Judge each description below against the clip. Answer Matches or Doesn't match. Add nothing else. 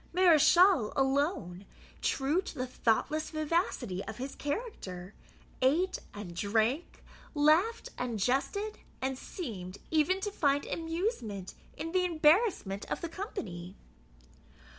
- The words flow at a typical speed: Doesn't match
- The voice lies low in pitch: Doesn't match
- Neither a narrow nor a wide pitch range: Doesn't match